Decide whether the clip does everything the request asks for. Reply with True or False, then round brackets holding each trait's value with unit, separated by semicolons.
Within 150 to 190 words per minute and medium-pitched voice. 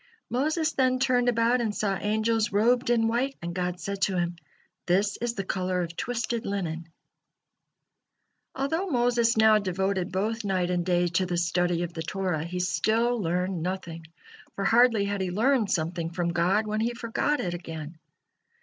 False (170 wpm; 195 Hz)